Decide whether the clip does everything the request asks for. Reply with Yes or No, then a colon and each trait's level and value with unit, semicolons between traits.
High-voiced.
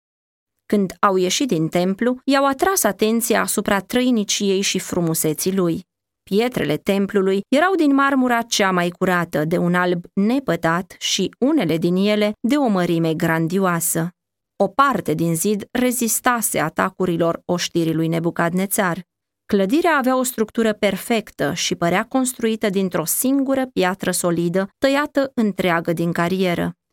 Yes: high, 195 Hz